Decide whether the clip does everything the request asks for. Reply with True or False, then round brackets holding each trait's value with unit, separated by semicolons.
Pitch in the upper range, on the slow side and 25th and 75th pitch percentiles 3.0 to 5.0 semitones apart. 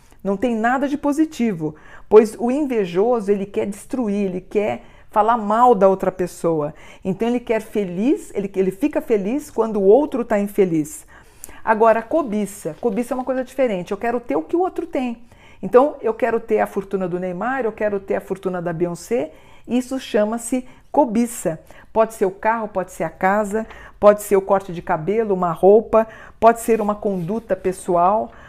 False (215 Hz; 180 wpm; 3.9 semitones)